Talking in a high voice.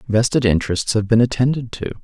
No: low, 115 Hz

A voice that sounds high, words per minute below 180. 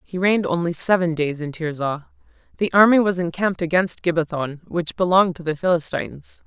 No: medium, 170 Hz; average, 165 wpm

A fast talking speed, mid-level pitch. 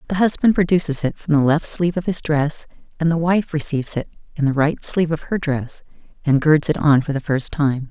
Yes: fast, 235 wpm; medium, 155 Hz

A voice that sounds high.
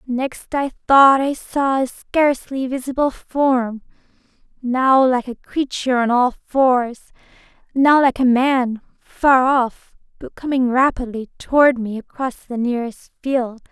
Yes: very high, 255 Hz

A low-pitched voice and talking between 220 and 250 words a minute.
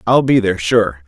Yes: low, 105 Hz; fast, 225 wpm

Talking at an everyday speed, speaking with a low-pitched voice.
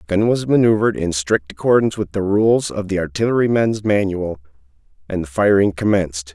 Yes: average, 170 wpm; low, 100 Hz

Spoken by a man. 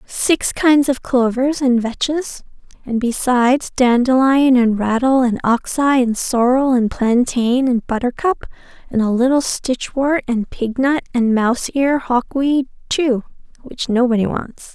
No: female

